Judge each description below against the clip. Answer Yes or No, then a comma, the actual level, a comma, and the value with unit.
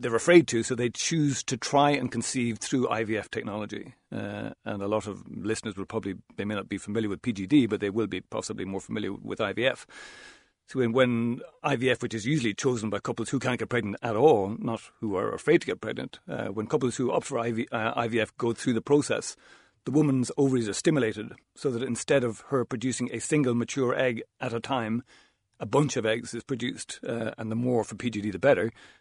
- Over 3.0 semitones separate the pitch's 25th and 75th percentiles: No, average, 2.7 semitones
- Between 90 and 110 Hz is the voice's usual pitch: No, low, 120 Hz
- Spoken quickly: Yes, fast, 215 wpm